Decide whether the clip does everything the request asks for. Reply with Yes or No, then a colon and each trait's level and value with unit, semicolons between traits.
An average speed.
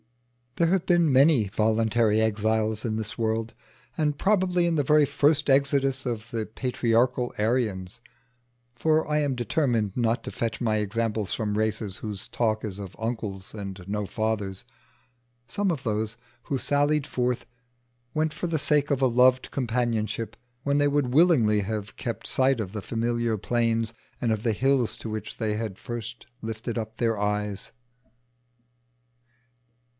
Yes: average, 155 wpm